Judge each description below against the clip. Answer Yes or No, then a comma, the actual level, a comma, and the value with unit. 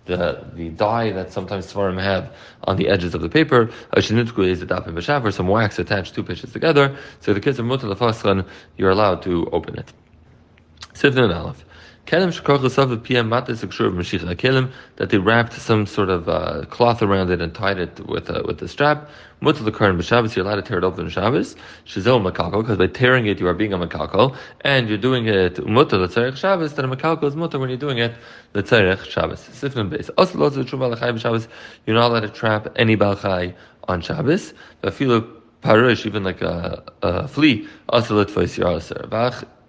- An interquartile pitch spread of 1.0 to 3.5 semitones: No, average, 4.7 semitones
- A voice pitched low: Yes, low, 110 Hz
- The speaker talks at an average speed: Yes, average, 175 wpm